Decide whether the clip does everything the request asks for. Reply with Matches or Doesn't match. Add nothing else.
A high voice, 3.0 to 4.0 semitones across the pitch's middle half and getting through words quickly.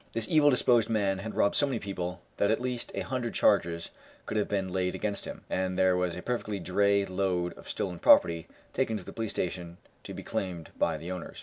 Doesn't match